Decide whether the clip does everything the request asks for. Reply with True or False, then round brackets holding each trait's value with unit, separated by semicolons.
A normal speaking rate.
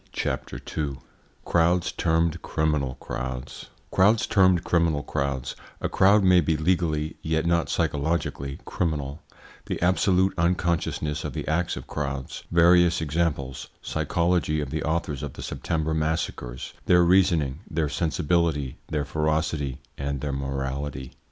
False (130 wpm)